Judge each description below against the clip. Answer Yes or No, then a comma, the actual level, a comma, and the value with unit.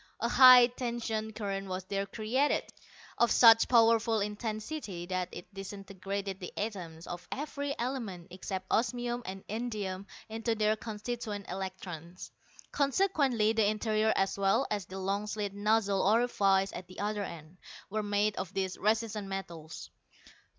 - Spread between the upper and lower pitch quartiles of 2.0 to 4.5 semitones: Yes, average, 2.8 semitones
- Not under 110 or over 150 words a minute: Yes, average, 140 wpm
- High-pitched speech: Yes, high, 210 Hz